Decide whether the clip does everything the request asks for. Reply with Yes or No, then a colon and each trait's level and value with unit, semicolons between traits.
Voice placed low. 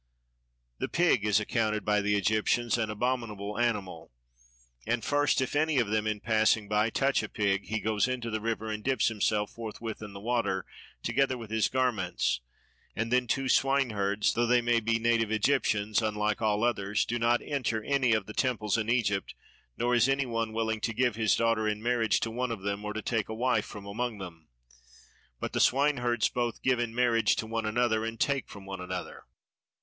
Yes: low, 110 Hz